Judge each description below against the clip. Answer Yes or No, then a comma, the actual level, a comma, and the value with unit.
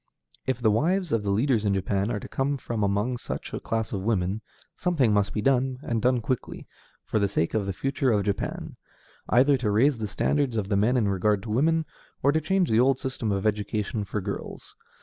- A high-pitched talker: No, low, 110 Hz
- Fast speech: Yes, fast, 220 wpm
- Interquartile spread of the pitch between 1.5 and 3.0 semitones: No, average, 4.3 semitones